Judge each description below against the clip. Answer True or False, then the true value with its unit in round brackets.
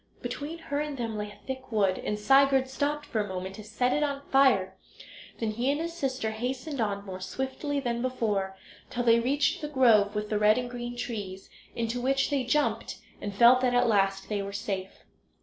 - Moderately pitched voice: False (240 Hz)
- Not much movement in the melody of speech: False (4.4 semitones)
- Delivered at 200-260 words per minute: True (205 wpm)